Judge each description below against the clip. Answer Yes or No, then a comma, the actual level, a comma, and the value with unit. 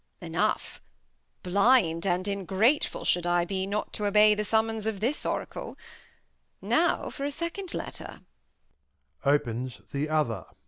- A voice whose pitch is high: Yes, high, 200 Hz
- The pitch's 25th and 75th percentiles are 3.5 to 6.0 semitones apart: Yes, average, 4.7 semitones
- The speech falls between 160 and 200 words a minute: No, slow, 135 wpm